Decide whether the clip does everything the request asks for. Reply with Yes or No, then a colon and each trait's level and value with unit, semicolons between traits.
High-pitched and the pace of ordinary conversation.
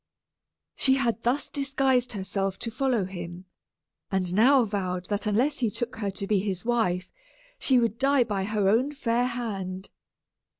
Yes: high, 220 Hz; average, 160 wpm